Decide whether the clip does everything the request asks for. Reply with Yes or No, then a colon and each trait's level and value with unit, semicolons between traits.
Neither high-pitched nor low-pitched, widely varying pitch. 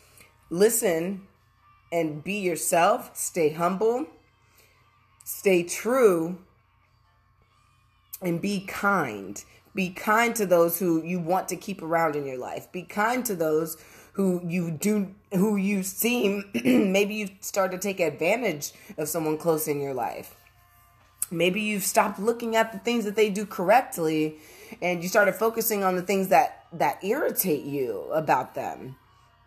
Yes: medium, 180 Hz; wide, 6.5 semitones